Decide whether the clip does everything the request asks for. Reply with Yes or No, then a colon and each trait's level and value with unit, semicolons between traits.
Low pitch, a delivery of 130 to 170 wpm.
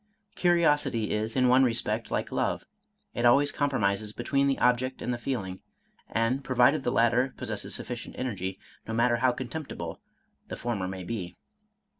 Yes: low, 120 Hz; average, 160 wpm